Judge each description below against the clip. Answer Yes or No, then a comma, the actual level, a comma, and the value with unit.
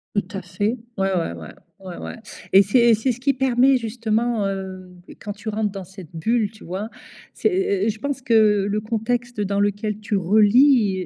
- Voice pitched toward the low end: No, high, 210 Hz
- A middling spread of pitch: Yes, average, 3.3 semitones